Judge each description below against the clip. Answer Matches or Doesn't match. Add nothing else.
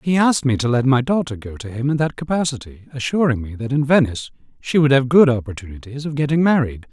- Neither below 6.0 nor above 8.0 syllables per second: Matches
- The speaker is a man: Matches